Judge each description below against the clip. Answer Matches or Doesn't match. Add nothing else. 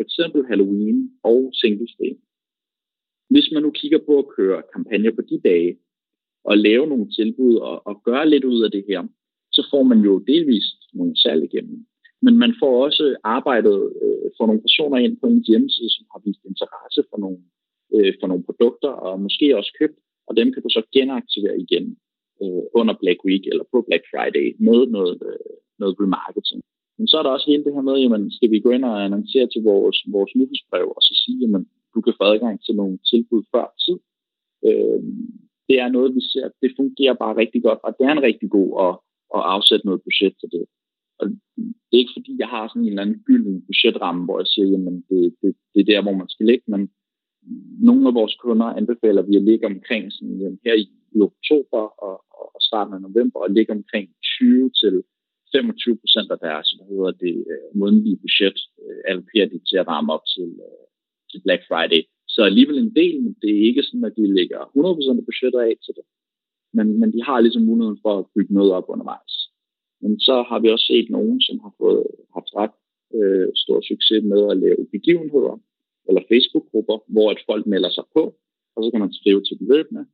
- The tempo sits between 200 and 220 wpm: Matches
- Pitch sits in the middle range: Matches